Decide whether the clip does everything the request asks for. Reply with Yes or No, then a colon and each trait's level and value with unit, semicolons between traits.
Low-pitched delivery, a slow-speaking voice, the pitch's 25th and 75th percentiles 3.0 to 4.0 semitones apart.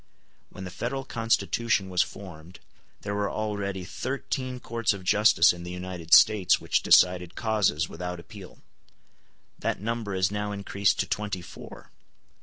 No: low, 100 Hz; average, 145 wpm; average, 3.3 semitones